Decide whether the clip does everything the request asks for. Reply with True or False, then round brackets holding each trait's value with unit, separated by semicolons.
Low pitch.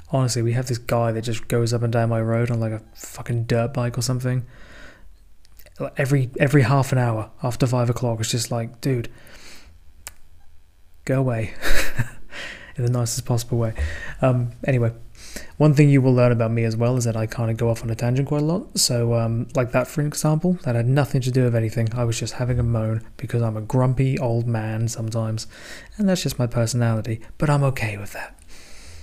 True (120 Hz)